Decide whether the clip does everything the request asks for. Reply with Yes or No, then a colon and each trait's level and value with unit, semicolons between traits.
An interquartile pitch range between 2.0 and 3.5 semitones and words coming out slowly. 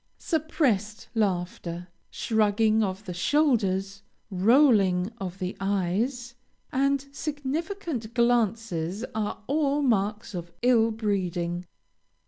No: average, 5.2 semitones; slow, 95 wpm